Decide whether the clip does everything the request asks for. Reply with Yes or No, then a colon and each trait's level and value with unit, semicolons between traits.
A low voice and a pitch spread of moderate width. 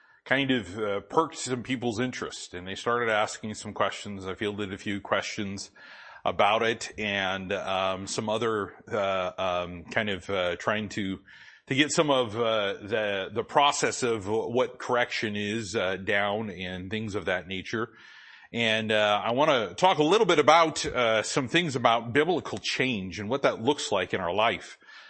Yes: low, 105 Hz; average, 3.5 semitones